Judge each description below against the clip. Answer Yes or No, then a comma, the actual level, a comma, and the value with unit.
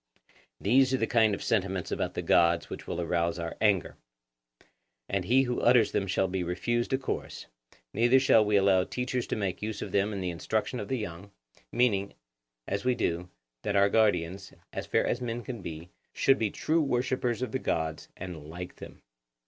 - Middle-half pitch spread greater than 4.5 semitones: Yes, average, 5.0 semitones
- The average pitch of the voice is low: Yes, low, 100 Hz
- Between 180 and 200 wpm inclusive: Yes, average, 195 wpm